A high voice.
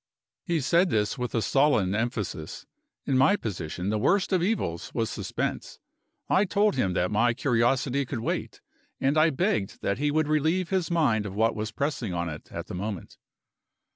No: low, 125 Hz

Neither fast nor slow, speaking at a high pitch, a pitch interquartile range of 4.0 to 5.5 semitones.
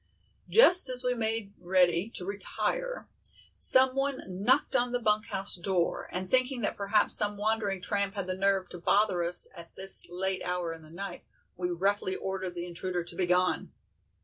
No: average, 175 wpm; high, 195 Hz; average, 3.5 semitones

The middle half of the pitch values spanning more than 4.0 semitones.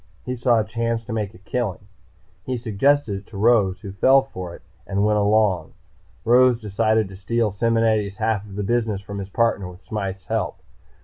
No: average, 2.9 semitones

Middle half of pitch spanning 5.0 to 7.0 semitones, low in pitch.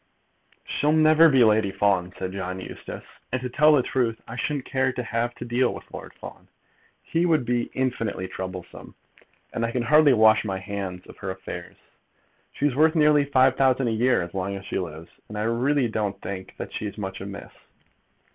Yes: average, 5.3 semitones; low, 115 Hz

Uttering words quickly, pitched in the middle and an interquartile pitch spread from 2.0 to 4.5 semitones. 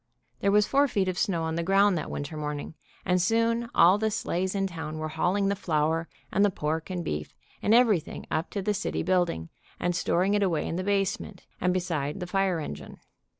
Yes: fast, 220 wpm; medium, 180 Hz; average, 3.8 semitones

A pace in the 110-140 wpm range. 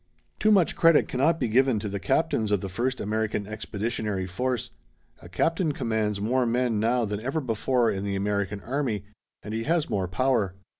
No: average, 185 wpm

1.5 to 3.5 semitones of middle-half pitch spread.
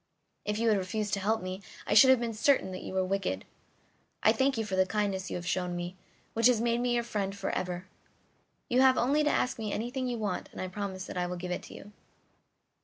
No: average, 4.1 semitones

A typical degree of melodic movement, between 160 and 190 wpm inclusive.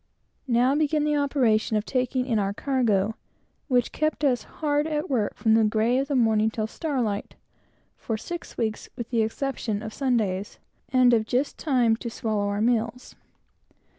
Yes: average, 3.9 semitones; average, 170 wpm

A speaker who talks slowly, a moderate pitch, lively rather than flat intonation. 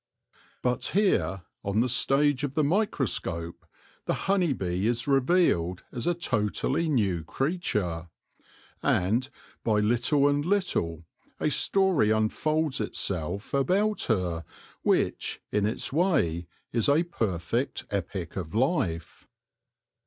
No: slow, 115 wpm; low, 120 Hz; wide, 8.7 semitones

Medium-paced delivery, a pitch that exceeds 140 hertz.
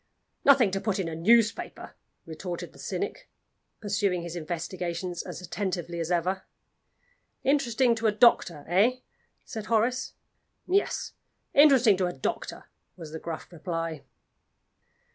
No: slow, 125 wpm; high, 190 Hz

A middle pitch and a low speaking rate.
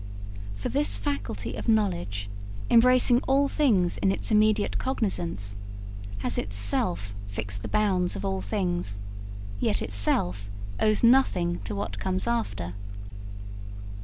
Yes: medium, 180 Hz; slow, 120 wpm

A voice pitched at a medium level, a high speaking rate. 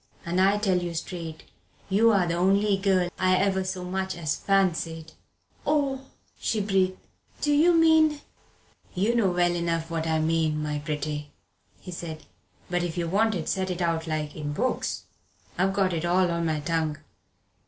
No: medium, 180 Hz; average, 170 wpm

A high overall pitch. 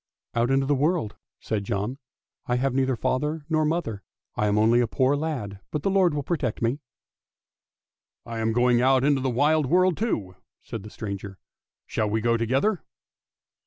No: low, 130 Hz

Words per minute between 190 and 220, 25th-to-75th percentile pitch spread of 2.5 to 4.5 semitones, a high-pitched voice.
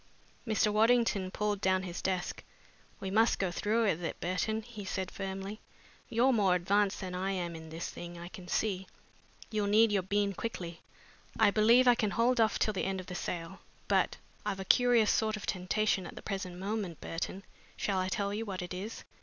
Yes: average, 195 wpm; average, 2.8 semitones; high, 195 Hz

